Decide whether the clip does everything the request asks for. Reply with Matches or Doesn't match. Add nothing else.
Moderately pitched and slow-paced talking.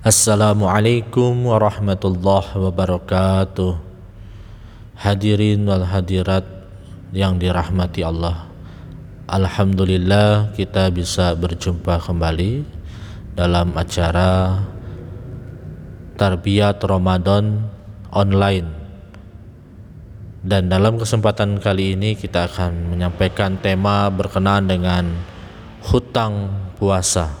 Doesn't match